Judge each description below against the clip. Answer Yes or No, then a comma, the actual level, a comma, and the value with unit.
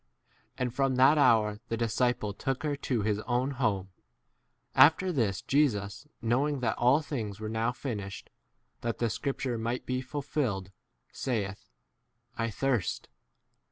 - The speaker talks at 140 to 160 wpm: Yes, average, 145 wpm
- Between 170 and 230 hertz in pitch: No, low, 120 Hz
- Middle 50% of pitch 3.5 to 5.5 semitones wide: Yes, average, 4.0 semitones